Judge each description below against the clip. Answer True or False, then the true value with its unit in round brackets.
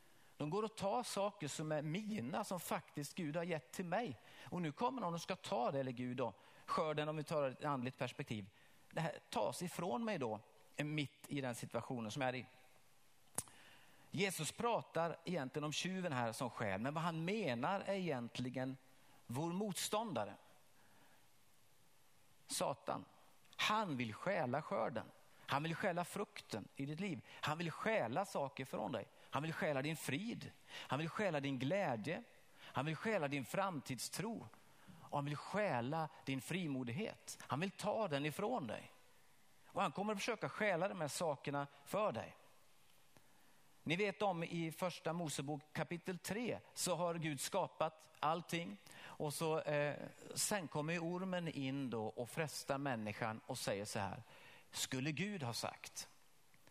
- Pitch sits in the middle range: True (155 Hz)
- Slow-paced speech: False (160 wpm)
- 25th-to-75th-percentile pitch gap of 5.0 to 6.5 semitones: True (5.4 semitones)